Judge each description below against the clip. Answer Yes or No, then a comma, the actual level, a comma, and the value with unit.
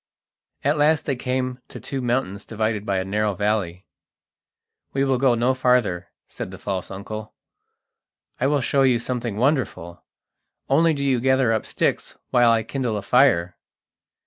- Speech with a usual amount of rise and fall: Yes, average, 4.4 semitones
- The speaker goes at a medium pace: Yes, average, 160 wpm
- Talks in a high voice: No, low, 120 Hz